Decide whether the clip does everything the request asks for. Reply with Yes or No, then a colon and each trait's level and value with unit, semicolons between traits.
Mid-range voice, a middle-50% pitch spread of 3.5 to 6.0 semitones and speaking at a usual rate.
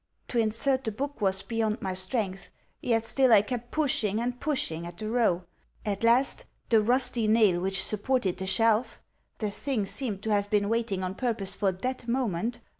No: high, 220 Hz; average, 3.9 semitones; average, 185 wpm